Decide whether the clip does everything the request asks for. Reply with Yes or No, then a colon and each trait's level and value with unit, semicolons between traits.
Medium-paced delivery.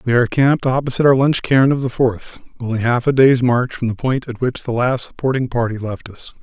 No: fast, 245 wpm